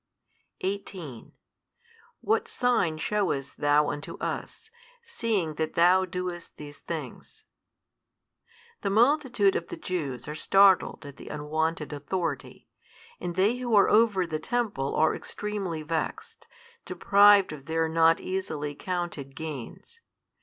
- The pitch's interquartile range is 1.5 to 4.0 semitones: No, average, 4.7 semitones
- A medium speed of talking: No, slow, 120 wpm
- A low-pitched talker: No, medium, 175 Hz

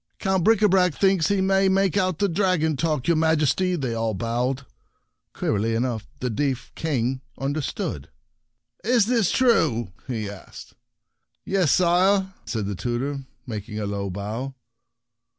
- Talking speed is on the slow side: No, average, 145 wpm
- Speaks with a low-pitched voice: No, medium, 145 Hz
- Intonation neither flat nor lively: No, wide, 8.5 semitones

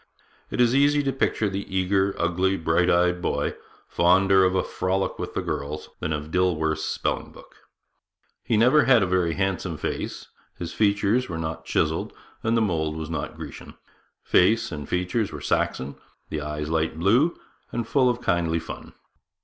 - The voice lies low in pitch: Yes, very low, 90 Hz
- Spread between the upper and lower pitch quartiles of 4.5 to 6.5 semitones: Yes, average, 4.8 semitones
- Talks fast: No, average, 170 wpm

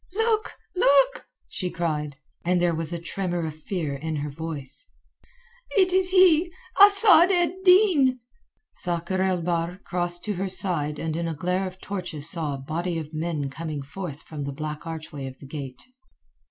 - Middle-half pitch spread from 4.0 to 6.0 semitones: Yes, average, 4.5 semitones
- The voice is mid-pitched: Yes, medium, 170 Hz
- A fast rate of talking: No, average, 165 wpm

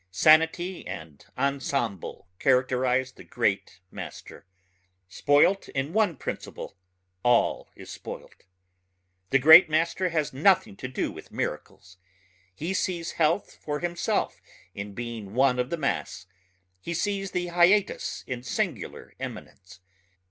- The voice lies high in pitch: No, medium, 140 Hz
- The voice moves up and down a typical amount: No, wide, 5.9 semitones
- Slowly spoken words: Yes, slow, 120 wpm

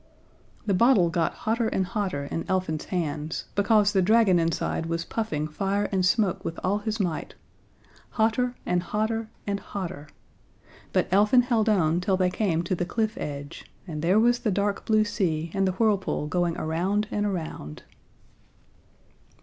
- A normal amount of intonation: Yes, average, 4.3 semitones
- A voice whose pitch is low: No, high, 190 Hz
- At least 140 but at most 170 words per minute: Yes, average, 160 wpm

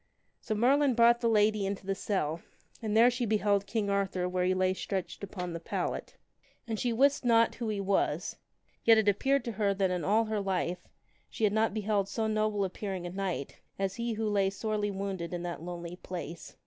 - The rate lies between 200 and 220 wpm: Yes, fast, 205 wpm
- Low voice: No, high, 200 Hz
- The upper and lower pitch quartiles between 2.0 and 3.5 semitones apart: Yes, average, 2.9 semitones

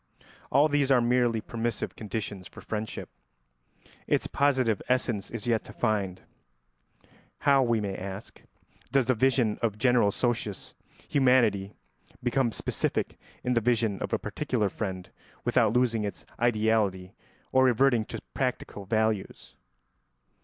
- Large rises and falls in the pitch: No, average, 3.2 semitones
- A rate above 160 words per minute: No, slow, 135 wpm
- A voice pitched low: Yes, low, 115 Hz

